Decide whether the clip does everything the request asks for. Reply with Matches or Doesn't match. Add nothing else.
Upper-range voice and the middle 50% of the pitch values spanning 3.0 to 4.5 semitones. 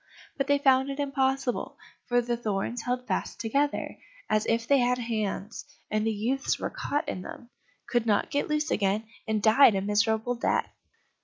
Matches